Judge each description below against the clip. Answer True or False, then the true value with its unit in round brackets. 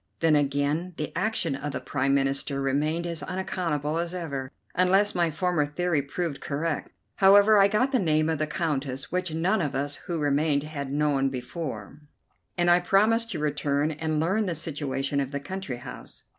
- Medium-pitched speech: True (155 Hz)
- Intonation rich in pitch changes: False (4.0 semitones)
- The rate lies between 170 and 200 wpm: True (180 wpm)